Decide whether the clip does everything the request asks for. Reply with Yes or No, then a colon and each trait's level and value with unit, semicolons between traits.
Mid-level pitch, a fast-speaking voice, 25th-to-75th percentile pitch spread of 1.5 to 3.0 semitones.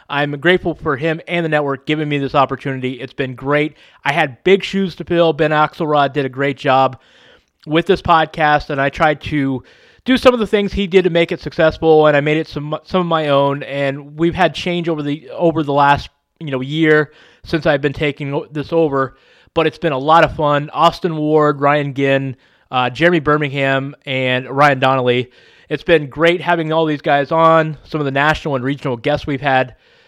Yes: medium, 150 Hz; fast, 210 wpm; average, 2.7 semitones